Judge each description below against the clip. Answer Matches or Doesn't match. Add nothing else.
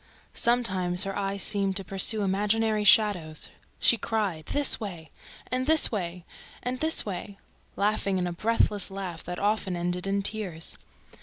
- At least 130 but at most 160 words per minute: Matches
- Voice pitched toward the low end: Doesn't match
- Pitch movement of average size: Matches